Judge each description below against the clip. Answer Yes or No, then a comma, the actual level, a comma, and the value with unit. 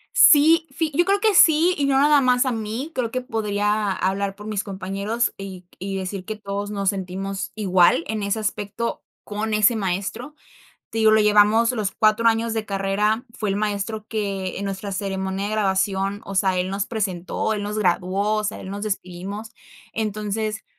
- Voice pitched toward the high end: Yes, high, 210 Hz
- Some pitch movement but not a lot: No, narrow, 2.3 semitones